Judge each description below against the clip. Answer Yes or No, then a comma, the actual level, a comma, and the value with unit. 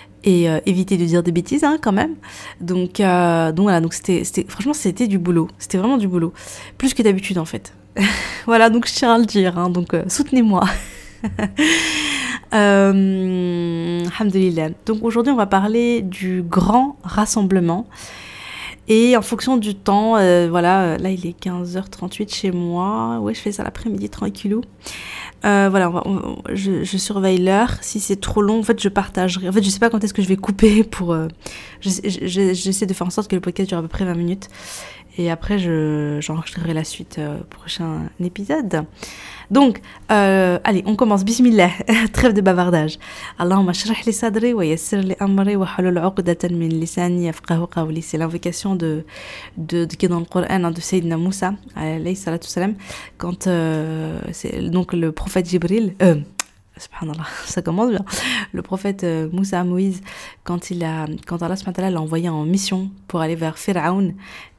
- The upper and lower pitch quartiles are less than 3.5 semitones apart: Yes, average, 3.1 semitones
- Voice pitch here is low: No, medium, 185 Hz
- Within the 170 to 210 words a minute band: Yes, average, 180 wpm